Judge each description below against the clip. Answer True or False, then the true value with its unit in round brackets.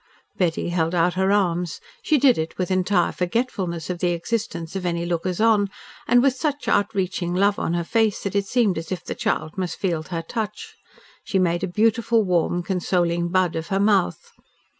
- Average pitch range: True (3.1 semitones)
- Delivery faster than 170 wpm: True (190 wpm)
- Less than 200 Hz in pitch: True (185 Hz)